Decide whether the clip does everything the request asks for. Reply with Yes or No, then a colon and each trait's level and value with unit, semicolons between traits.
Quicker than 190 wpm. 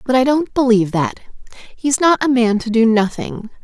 Yes: average, 200 wpm